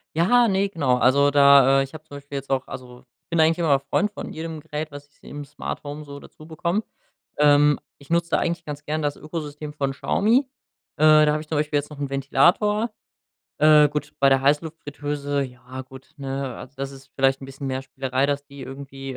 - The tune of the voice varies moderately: No, narrow, 2.2 semitones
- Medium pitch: Yes, medium, 145 Hz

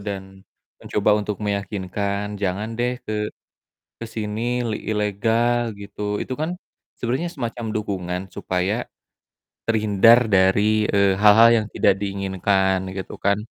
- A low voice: Yes, low, 105 Hz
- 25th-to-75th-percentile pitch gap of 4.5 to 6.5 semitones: No, narrow, 2.5 semitones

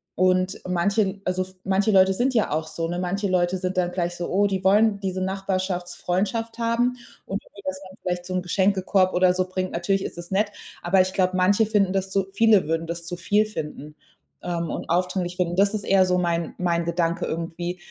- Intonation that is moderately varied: No, narrow, 1.9 semitones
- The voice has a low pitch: No, medium, 185 Hz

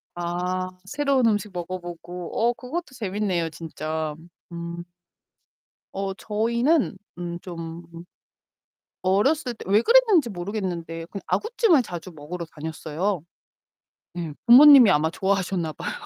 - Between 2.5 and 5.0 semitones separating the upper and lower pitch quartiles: No, wide, 5.6 semitones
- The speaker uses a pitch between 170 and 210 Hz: Yes, medium, 185 Hz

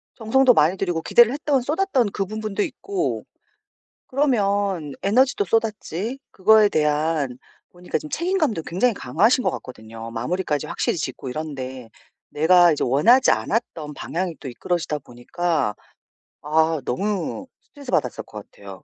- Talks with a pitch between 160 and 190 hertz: Yes, medium, 185 Hz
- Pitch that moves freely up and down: Yes, wide, 8.1 semitones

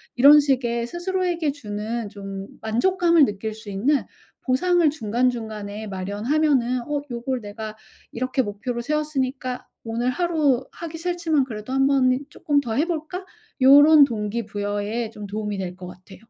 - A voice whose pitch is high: Yes, very high, 250 Hz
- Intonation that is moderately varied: No, wide, 5.7 semitones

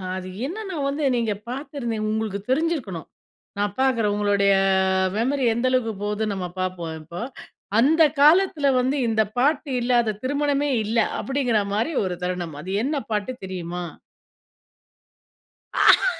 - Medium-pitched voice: No, high, 230 Hz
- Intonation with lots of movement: Yes, wide, 5.8 semitones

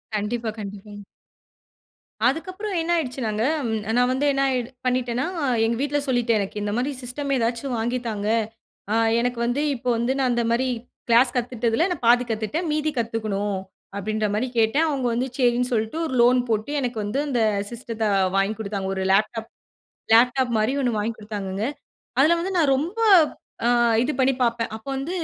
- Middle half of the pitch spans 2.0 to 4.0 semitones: Yes, average, 3.3 semitones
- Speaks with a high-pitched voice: Yes, high, 240 Hz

